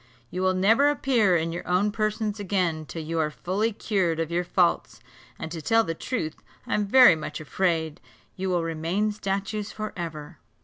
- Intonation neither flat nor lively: Yes, average, 4.2 semitones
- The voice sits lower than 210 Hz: Yes, medium, 185 Hz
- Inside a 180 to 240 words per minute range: Yes, average, 185 wpm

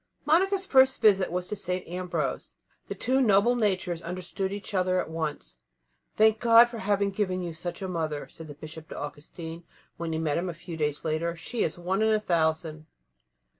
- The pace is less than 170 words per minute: No, average, 195 wpm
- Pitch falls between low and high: Yes, medium, 180 Hz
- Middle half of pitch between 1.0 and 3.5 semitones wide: No, average, 4.5 semitones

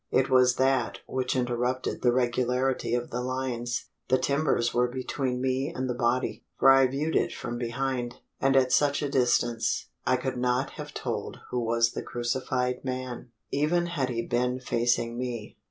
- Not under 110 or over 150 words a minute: No, average, 170 wpm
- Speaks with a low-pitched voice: Yes, low, 125 Hz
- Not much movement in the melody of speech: Yes, narrow, 1.5 semitones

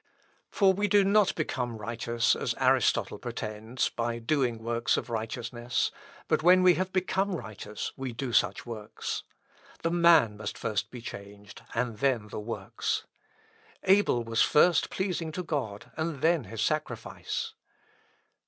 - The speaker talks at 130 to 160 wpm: Yes, average, 145 wpm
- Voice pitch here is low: Yes, low, 120 Hz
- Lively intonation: Yes, wide, 7.0 semitones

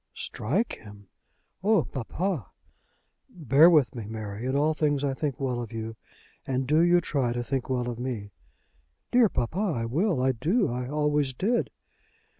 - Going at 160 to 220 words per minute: Yes, average, 165 wpm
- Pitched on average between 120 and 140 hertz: Yes, low, 135 Hz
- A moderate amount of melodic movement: Yes, average, 4.8 semitones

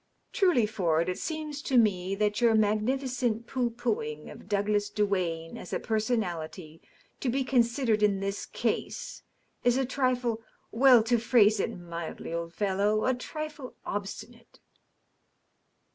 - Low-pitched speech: No, high, 220 Hz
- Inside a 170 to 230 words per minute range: No, average, 145 wpm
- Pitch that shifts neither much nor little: Yes, average, 4.1 semitones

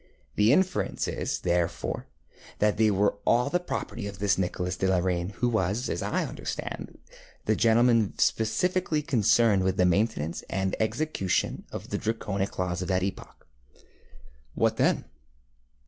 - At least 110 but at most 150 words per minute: Yes, average, 145 wpm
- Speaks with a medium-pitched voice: No, low, 100 Hz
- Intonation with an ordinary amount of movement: Yes, average, 3.9 semitones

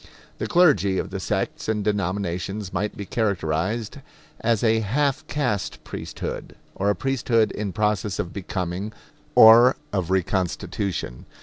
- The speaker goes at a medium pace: No, slow, 130 wpm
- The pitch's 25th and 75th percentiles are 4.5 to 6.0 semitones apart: No, average, 3.0 semitones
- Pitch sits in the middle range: No, low, 105 Hz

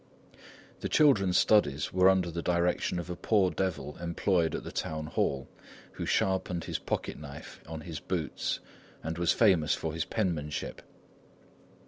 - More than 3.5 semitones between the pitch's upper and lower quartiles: No, average, 3.0 semitones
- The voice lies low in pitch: Yes, very low, 85 Hz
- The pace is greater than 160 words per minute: No, average, 145 wpm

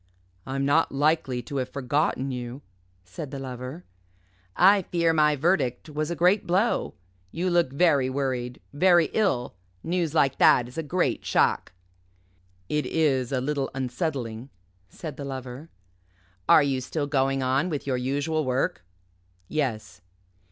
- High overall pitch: No, medium, 140 Hz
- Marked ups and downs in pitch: No, average, 3.9 semitones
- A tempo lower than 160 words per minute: Yes, average, 145 wpm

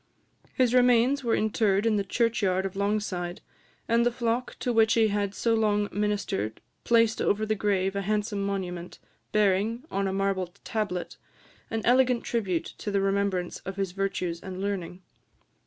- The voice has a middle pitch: No, high, 205 Hz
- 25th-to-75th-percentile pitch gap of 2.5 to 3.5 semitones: Yes, average, 2.8 semitones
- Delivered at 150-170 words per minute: Yes, average, 160 wpm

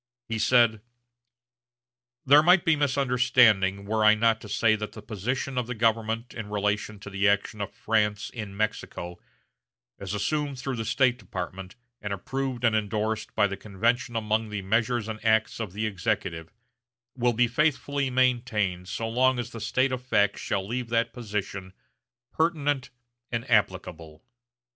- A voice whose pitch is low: Yes, low, 110 Hz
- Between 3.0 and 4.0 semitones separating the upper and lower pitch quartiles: Yes, average, 3.4 semitones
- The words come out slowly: No, average, 160 wpm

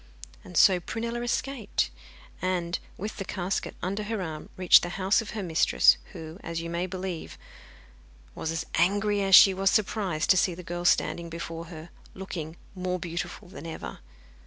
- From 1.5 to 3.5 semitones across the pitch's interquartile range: Yes, narrow, 2.6 semitones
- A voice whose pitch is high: No, medium, 180 Hz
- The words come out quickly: No, average, 170 wpm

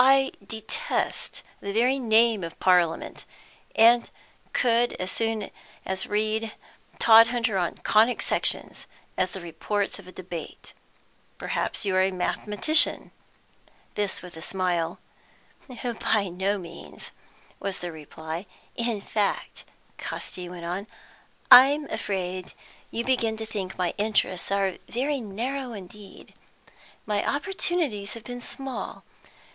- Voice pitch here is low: No, high, 210 Hz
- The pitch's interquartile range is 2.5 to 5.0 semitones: Yes, average, 4.2 semitones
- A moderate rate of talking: No, slow, 120 wpm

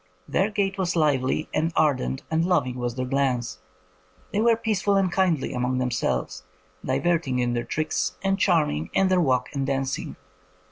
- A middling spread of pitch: No, wide, 6.5 semitones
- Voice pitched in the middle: Yes, medium, 150 Hz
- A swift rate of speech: No, average, 175 wpm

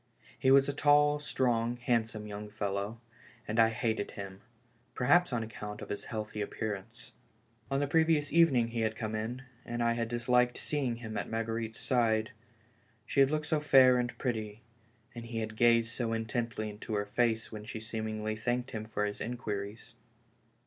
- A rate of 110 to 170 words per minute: No, average, 185 wpm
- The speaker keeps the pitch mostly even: Yes, narrow, 2.3 semitones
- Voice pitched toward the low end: Yes, low, 115 Hz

